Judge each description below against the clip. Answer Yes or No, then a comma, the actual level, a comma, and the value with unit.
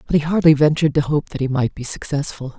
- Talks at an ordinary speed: No, fast, 255 wpm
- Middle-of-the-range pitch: Yes, medium, 145 Hz